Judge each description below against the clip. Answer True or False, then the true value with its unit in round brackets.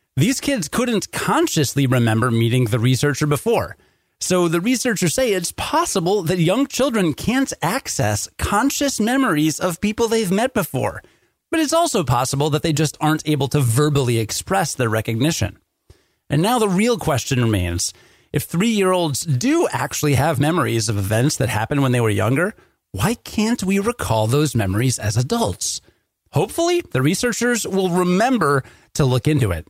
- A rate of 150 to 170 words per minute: True (160 wpm)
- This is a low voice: False (155 Hz)